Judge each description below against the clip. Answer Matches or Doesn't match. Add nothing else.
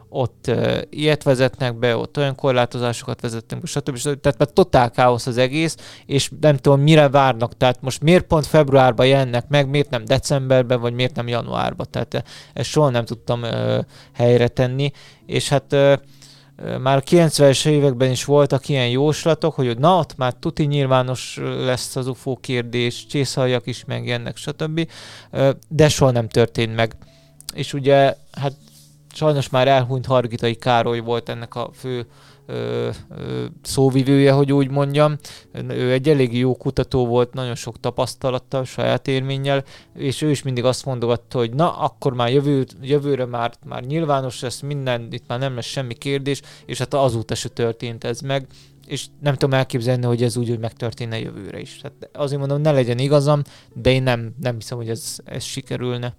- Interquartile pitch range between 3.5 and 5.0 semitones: Doesn't match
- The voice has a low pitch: Matches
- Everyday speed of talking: Doesn't match